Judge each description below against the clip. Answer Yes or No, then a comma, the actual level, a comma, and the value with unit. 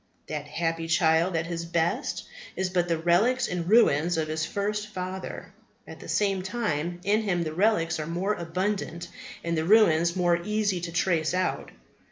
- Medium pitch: Yes, medium, 175 Hz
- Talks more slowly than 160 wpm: No, average, 175 wpm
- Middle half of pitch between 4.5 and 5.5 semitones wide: No, average, 3.2 semitones